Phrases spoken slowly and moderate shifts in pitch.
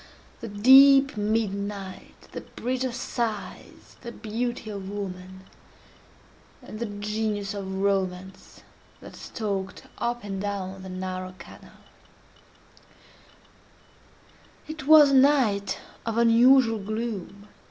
Yes: slow, 105 wpm; average, 3.5 semitones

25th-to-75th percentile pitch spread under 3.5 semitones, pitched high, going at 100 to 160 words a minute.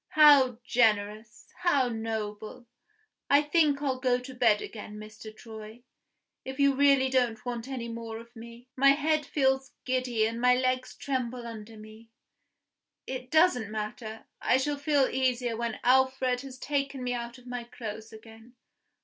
Yes: average, 2.9 semitones; high, 245 Hz; average, 155 wpm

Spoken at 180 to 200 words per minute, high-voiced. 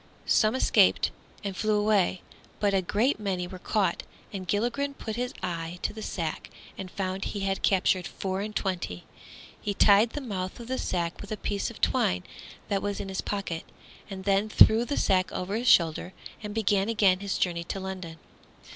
Yes: average, 190 wpm; high, 195 Hz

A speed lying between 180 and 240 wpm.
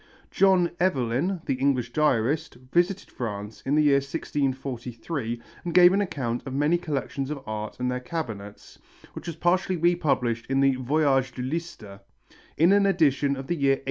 No: average, 170 wpm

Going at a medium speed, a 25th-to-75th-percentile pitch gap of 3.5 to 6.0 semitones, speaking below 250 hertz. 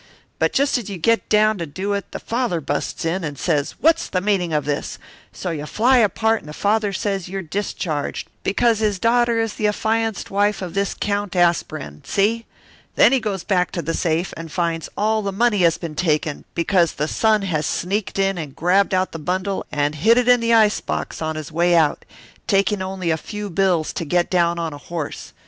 No: fast, 210 wpm; average, 4.3 semitones; high, 190 Hz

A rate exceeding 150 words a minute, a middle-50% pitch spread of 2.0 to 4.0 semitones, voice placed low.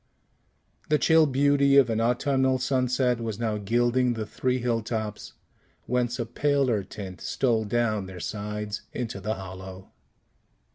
No: average, 140 wpm; average, 3.4 semitones; low, 120 Hz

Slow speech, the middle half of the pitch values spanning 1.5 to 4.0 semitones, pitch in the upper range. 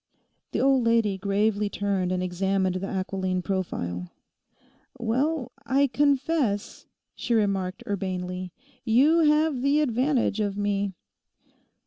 No: slow, 110 wpm; wide, 5.6 semitones; high, 205 Hz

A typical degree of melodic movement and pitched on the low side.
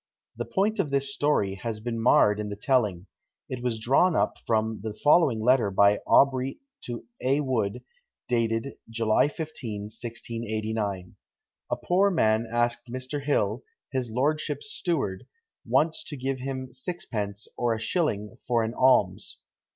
Yes: average, 4.0 semitones; low, 120 Hz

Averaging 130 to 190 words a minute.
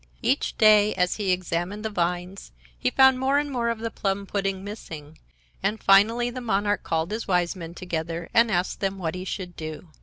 No: average, 200 wpm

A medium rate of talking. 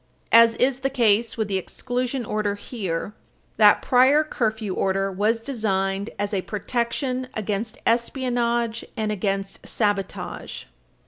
No: slow, 125 wpm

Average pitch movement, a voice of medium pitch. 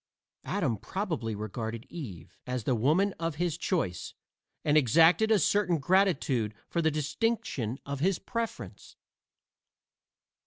No: wide, 7.8 semitones; medium, 150 Hz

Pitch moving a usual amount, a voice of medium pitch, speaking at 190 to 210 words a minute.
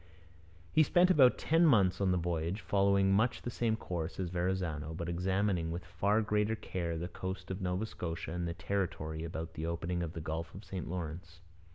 No: average, 3.1 semitones; very low, 90 Hz; average, 195 wpm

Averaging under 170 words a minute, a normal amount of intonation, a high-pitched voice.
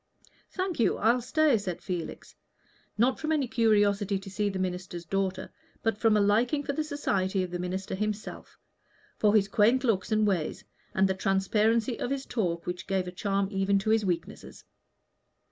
No: average, 180 wpm; average, 3.3 semitones; high, 205 Hz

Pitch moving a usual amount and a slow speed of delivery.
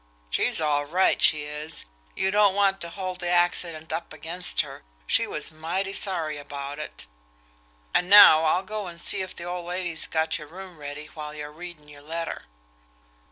No: average, 3.3 semitones; average, 180 wpm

